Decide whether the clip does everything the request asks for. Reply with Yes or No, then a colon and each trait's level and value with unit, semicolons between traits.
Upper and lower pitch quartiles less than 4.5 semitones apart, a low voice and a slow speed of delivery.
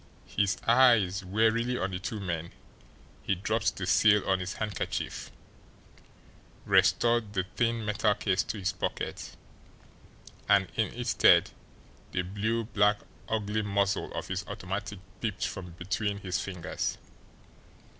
Yes: narrow, 2.6 semitones; low, 100 Hz; slow, 130 wpm